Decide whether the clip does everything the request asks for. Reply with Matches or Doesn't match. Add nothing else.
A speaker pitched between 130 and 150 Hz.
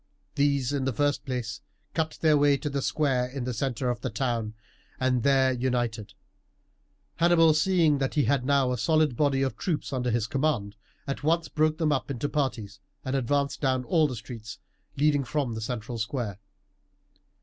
Matches